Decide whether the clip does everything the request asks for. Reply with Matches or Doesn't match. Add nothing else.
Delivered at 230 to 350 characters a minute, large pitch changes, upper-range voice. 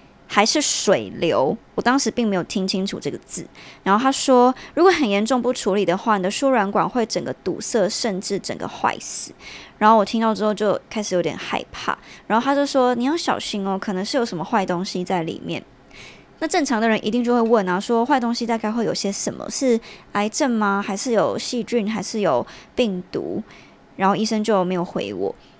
Doesn't match